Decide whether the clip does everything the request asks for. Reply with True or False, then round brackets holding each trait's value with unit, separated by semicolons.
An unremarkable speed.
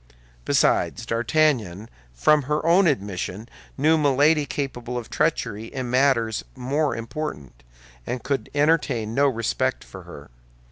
False (125 wpm)